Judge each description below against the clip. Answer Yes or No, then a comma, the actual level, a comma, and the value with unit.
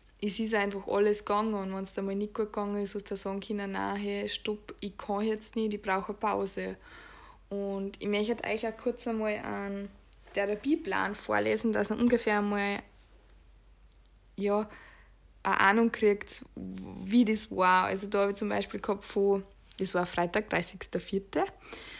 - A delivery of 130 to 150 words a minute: No, average, 175 wpm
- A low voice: No, high, 205 Hz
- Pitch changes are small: Yes, narrow, 1.6 semitones